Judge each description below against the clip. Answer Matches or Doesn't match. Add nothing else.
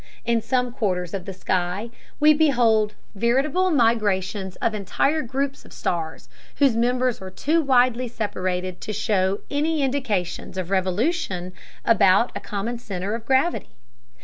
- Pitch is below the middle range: Doesn't match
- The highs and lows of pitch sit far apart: Matches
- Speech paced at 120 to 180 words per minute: Matches